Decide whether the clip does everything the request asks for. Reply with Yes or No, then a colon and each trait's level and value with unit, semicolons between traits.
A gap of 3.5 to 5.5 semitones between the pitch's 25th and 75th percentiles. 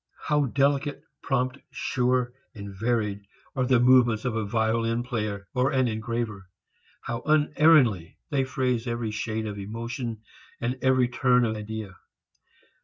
No: average, 2.9 semitones